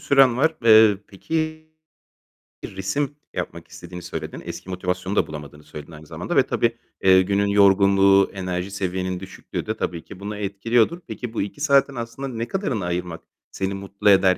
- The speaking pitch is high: No, low, 100 Hz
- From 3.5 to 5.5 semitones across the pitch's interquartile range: Yes, average, 4.1 semitones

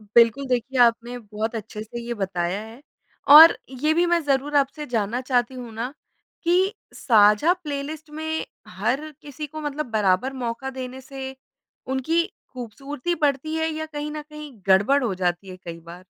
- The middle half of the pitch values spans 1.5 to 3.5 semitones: No, average, 5.2 semitones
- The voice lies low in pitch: No, very high, 265 Hz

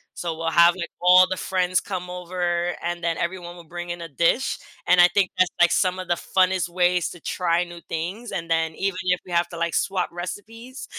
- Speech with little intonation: Yes, narrow, 1.2 semitones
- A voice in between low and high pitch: Yes, medium, 175 Hz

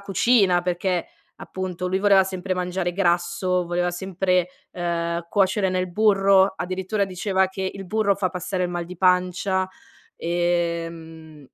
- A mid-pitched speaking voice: Yes, medium, 180 Hz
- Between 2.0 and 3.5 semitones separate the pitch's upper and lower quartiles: No, narrow, 1.6 semitones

